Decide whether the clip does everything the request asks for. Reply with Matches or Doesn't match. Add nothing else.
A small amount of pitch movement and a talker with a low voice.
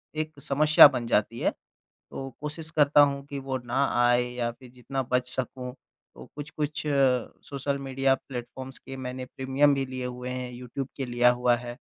Matches